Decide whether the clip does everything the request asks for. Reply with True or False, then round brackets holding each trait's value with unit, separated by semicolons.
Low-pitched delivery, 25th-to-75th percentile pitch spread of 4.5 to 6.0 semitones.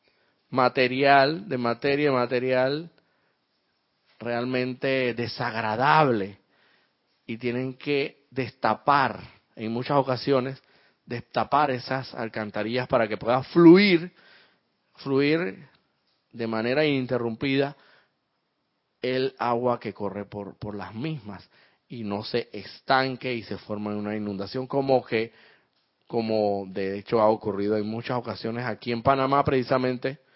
False (125 Hz; 3.6 semitones)